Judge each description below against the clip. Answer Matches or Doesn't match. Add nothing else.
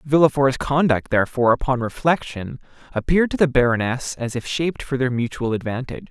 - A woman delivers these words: Doesn't match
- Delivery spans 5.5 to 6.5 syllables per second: Matches